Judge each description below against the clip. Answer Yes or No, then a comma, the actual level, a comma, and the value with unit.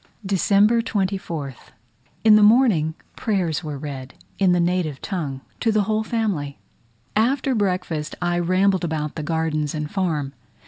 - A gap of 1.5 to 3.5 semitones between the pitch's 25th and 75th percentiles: No, average, 5.2 semitones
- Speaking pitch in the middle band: Yes, medium, 180 Hz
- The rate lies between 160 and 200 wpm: No, average, 140 wpm